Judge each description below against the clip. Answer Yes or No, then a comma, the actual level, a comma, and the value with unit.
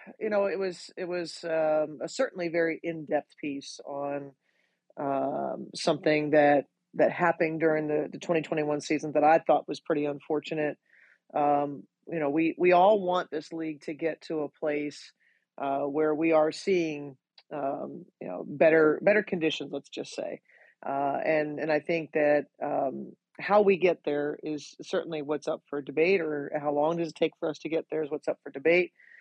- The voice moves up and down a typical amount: No, narrow, 2.2 semitones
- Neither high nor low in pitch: Yes, medium, 155 Hz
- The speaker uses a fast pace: No, average, 185 wpm